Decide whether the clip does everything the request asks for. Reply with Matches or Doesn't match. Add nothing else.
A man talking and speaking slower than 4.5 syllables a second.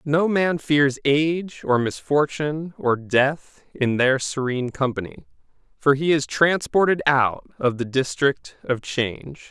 Matches